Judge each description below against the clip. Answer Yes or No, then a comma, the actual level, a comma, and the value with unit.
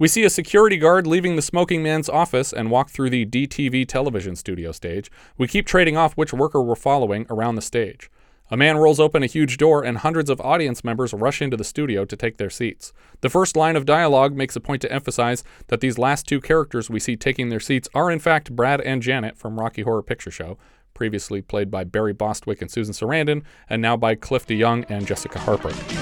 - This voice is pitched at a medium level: No, low, 130 Hz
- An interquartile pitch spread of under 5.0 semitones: No, wide, 5.4 semitones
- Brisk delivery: Yes, fast, 220 wpm